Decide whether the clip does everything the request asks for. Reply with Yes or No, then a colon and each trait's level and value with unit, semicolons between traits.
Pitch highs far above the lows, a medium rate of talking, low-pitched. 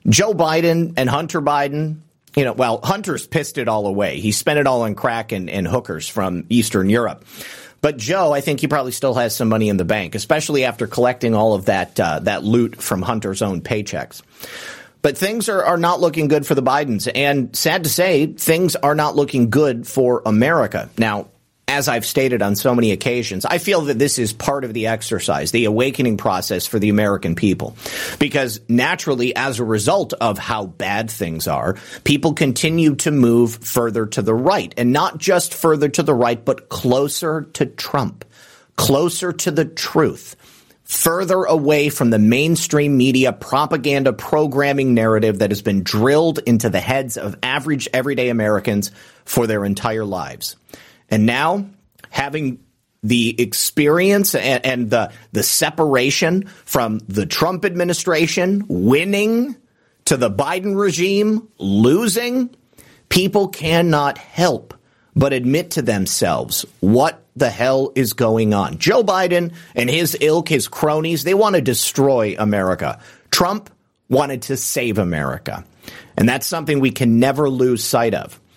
Yes: wide, 5.7 semitones; average, 160 wpm; low, 130 Hz